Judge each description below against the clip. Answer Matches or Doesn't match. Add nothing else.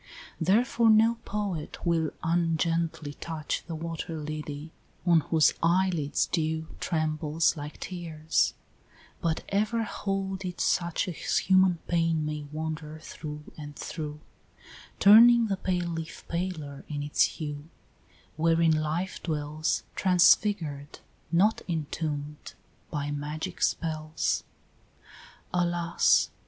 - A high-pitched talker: Doesn't match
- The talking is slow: Matches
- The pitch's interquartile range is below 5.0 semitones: Matches